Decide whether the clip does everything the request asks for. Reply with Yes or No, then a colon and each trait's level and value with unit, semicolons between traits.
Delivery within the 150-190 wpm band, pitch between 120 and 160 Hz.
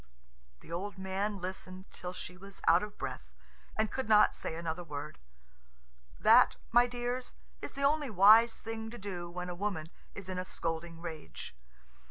No: average, 170 wpm; high, 190 Hz